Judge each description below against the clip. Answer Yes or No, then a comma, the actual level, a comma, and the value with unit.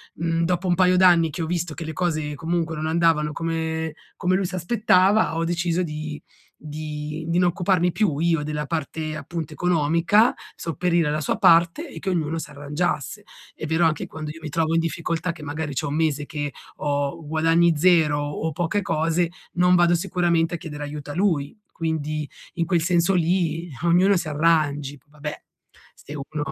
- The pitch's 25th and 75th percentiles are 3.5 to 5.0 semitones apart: No, narrow, 2.4 semitones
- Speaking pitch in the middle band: Yes, medium, 165 Hz